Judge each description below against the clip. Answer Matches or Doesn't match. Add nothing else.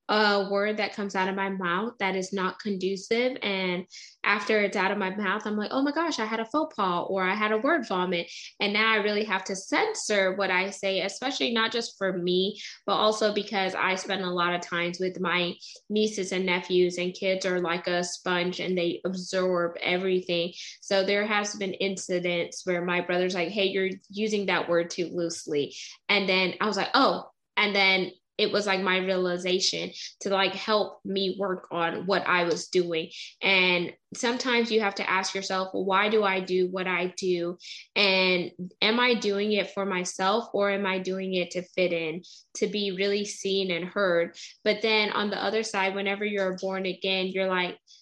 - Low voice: Doesn't match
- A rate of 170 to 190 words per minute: Doesn't match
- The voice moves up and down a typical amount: Doesn't match